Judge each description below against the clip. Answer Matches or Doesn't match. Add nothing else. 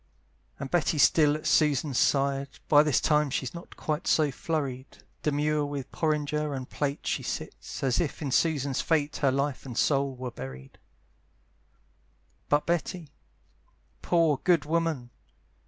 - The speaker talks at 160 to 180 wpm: Doesn't match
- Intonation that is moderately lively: Doesn't match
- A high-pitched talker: Doesn't match